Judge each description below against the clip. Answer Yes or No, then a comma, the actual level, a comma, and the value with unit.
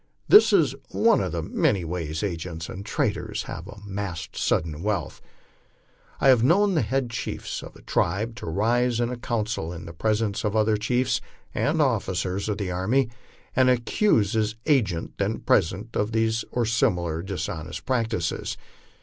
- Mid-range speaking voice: No, low, 105 Hz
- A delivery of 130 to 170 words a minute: Yes, average, 165 wpm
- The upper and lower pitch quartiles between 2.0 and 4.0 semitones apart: No, average, 4.9 semitones